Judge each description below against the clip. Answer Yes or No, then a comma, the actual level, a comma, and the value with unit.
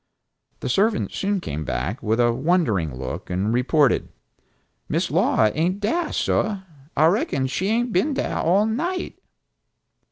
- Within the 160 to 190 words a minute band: No, average, 140 wpm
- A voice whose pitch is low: No, medium, 160 Hz